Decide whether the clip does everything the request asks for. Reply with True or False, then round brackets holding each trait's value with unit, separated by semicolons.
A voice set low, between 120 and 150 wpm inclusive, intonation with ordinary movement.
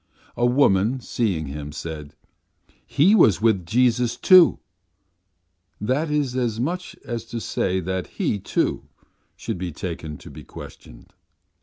False (115 Hz; 135 wpm; 6.2 semitones)